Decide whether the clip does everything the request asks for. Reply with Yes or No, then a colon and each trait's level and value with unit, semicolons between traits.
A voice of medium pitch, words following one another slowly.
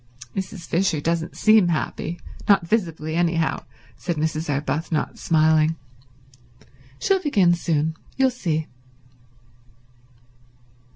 Yes: medium, 165 Hz; slow, 90 wpm